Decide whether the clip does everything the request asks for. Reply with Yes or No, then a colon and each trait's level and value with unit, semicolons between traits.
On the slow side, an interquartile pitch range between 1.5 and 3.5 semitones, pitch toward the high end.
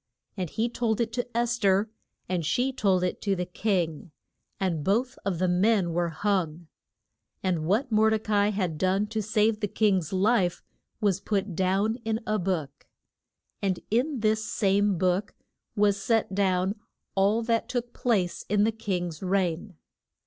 No: average, 165 wpm; average, 3.2 semitones; high, 200 Hz